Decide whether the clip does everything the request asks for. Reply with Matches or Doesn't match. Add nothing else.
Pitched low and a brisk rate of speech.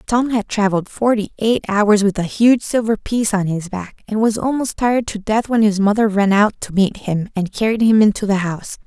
Doesn't match